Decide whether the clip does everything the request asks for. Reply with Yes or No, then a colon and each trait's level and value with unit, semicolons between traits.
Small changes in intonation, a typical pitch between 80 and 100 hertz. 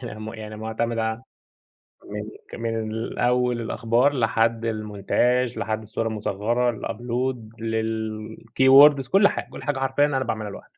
No: narrow, 2.2 semitones; low, 115 Hz